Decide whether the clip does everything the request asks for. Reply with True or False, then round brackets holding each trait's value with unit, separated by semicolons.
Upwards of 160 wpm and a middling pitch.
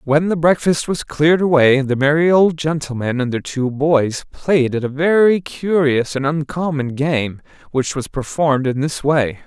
True (175 wpm; 145 Hz)